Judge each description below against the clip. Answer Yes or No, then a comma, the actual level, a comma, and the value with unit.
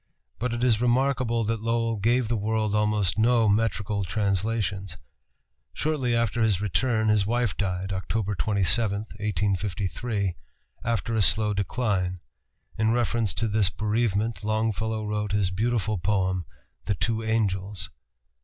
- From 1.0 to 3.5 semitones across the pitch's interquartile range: Yes, narrow, 2.4 semitones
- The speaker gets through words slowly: Yes, slow, 130 wpm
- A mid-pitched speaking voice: No, low, 105 Hz